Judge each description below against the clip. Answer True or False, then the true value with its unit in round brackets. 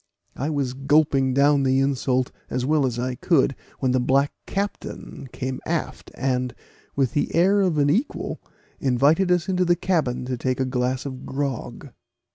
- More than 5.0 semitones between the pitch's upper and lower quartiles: False (3.3 semitones)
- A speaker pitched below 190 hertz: True (135 Hz)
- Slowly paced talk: False (170 wpm)